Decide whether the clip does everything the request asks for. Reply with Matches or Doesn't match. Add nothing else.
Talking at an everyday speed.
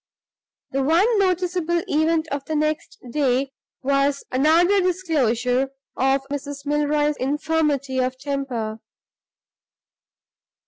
Doesn't match